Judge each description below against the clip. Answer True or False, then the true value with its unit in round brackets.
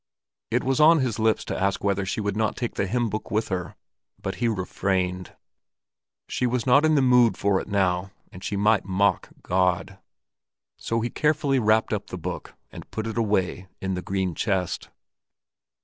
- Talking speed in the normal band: True (185 wpm)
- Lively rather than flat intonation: False (3.7 semitones)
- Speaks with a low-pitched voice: True (105 Hz)